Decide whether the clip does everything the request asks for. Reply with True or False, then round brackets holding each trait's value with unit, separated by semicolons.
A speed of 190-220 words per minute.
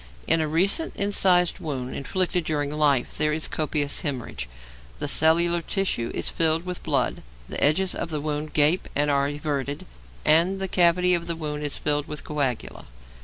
False (170 wpm)